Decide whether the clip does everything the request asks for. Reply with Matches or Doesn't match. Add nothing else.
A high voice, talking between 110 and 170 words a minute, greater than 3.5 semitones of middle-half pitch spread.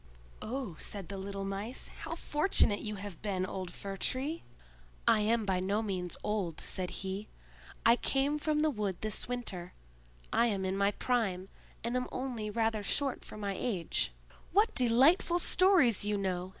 Matches